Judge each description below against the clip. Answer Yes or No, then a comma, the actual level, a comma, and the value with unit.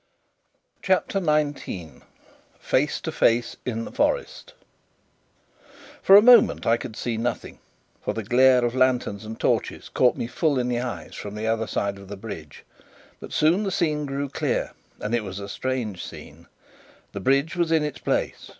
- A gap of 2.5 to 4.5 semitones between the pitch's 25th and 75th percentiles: No, average, 5.3 semitones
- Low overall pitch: Yes, low, 125 Hz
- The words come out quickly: No, average, 170 wpm